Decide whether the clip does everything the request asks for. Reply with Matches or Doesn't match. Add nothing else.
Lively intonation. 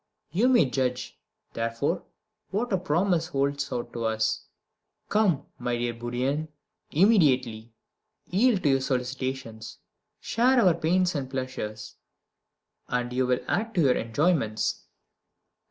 Matches